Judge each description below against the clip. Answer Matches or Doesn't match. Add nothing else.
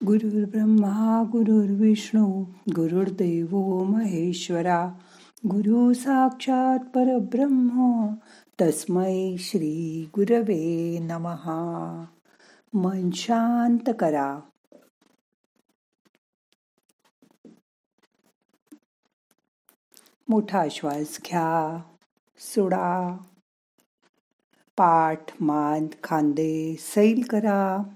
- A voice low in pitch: Doesn't match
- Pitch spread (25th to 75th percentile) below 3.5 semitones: Doesn't match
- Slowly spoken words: Matches